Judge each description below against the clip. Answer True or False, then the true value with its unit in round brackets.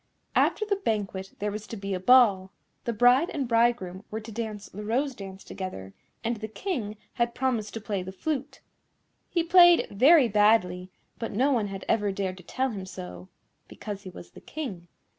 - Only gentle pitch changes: False (4.3 semitones)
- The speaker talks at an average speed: True (190 wpm)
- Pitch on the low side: False (215 Hz)